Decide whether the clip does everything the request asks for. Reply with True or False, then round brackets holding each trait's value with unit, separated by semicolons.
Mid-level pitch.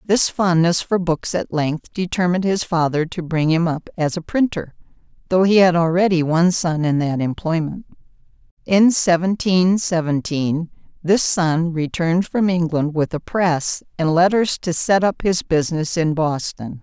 True (170 Hz)